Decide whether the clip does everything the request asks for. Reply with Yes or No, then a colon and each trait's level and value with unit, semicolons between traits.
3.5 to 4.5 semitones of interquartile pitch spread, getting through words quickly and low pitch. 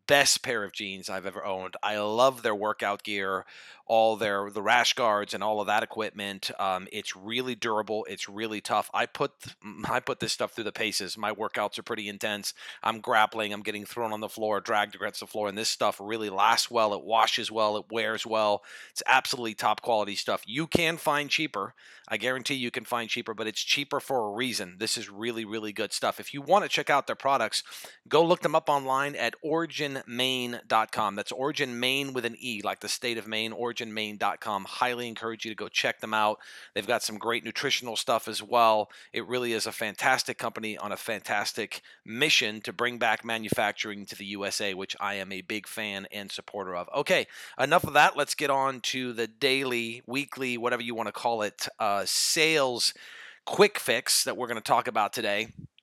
No: average, 3.1 semitones; fast, 210 wpm; low, 110 Hz